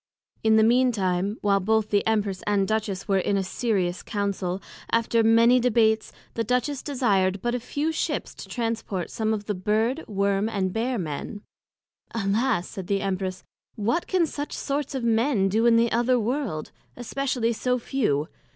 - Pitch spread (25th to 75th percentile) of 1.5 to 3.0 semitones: No, average, 3.5 semitones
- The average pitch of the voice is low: No, high, 220 Hz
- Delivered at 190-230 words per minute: No, average, 170 wpm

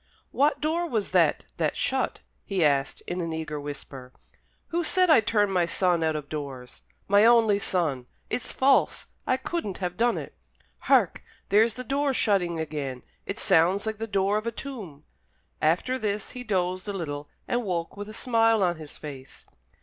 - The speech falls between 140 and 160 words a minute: No, average, 180 wpm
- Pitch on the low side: No, high, 195 Hz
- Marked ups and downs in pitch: Yes, wide, 6.2 semitones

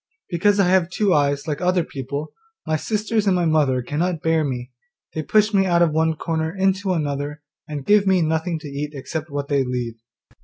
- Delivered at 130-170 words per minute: No, average, 200 wpm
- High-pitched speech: No, medium, 160 Hz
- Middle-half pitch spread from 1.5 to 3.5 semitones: No, average, 4.2 semitones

